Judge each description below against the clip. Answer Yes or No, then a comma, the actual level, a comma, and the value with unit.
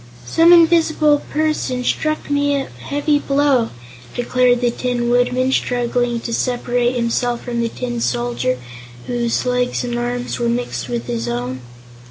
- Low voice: No, high, 245 Hz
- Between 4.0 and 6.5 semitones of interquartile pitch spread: No, narrow, 2.4 semitones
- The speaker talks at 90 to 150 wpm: Yes, average, 145 wpm